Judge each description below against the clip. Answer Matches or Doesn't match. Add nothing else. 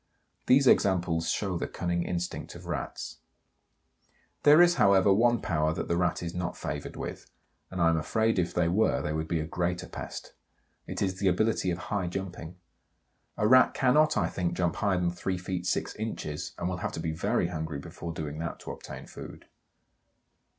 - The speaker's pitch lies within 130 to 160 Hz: Doesn't match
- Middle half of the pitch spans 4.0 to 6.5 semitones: Doesn't match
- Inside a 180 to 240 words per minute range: Matches